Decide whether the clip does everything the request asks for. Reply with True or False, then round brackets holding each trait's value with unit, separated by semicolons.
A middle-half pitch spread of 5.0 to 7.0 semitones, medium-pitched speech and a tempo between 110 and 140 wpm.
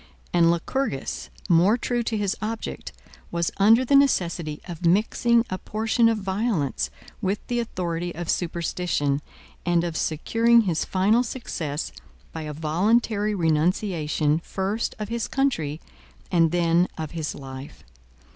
True (5.4 semitones; 180 Hz; 135 wpm)